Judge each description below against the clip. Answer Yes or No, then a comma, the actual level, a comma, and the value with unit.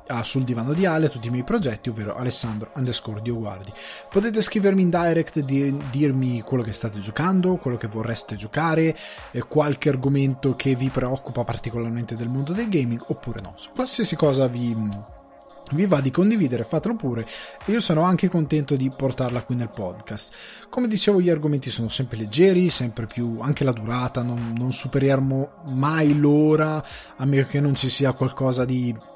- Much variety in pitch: No, average, 4.5 semitones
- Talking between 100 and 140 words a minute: No, fast, 170 wpm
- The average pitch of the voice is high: No, low, 135 Hz